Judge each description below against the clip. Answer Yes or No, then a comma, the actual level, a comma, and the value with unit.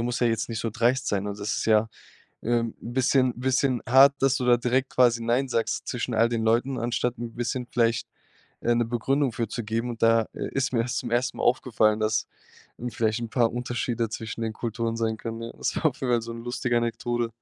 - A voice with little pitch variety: Yes, narrow, 1.4 semitones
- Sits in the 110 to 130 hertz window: Yes, low, 120 Hz